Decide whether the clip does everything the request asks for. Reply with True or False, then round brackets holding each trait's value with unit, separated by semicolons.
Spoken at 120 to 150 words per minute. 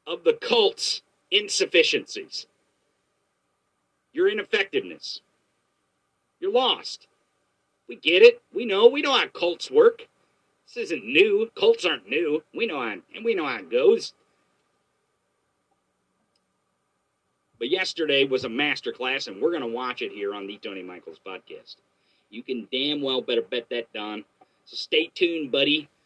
True (140 wpm)